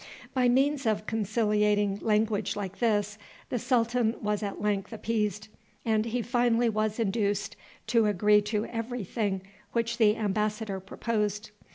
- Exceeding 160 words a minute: No, average, 140 wpm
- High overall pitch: Yes, high, 215 Hz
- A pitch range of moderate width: No, narrow, 1.8 semitones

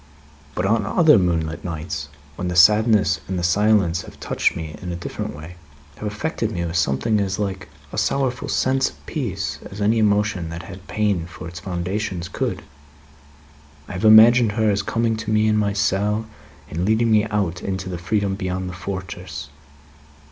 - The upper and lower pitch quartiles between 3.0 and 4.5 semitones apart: Yes, average, 3.5 semitones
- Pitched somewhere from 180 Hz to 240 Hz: No, low, 100 Hz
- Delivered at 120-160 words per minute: No, average, 180 wpm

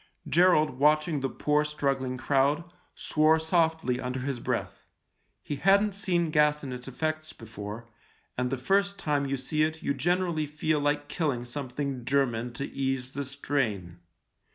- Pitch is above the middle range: No, medium, 145 Hz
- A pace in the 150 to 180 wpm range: Yes, average, 155 wpm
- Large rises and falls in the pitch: No, average, 3.3 semitones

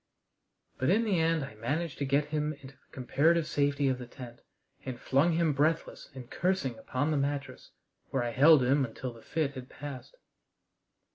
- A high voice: No, medium, 140 Hz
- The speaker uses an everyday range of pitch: Yes, average, 3.4 semitones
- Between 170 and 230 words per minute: Yes, average, 185 wpm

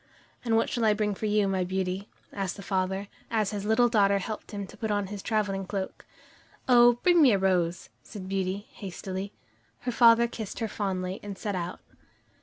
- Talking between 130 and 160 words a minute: No, average, 195 wpm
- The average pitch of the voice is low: No, high, 200 Hz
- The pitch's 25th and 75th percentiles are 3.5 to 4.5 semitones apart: No, narrow, 2.5 semitones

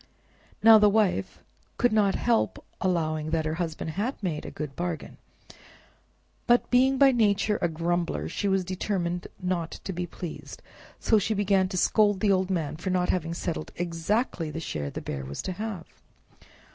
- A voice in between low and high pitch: Yes, medium, 180 Hz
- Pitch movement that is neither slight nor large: Yes, average, 4.0 semitones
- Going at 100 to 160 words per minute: No, average, 170 wpm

